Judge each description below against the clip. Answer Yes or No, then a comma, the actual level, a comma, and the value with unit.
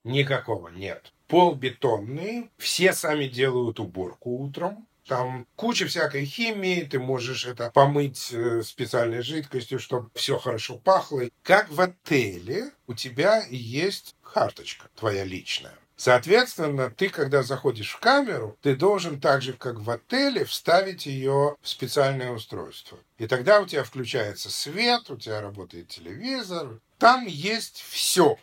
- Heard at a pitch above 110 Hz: Yes, low, 135 Hz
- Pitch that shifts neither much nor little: No, wide, 6.6 semitones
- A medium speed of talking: Yes, average, 130 wpm